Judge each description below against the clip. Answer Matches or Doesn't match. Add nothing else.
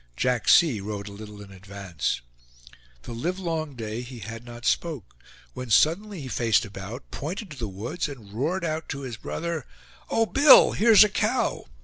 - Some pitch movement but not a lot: Doesn't match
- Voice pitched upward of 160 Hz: Doesn't match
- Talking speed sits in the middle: Matches